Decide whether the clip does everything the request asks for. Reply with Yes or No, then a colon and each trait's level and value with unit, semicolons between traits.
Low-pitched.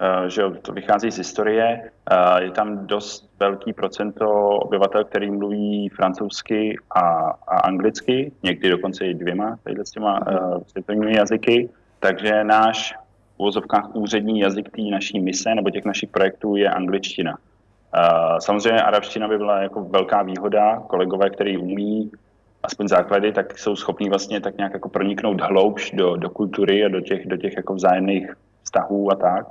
Yes: low, 105 Hz